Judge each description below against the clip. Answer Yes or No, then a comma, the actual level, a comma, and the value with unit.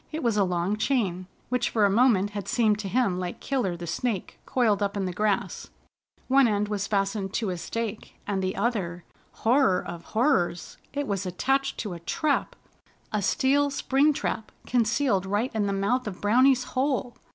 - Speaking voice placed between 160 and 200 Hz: No, high, 210 Hz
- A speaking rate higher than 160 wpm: Yes, average, 185 wpm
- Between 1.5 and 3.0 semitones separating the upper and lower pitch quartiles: No, average, 4.7 semitones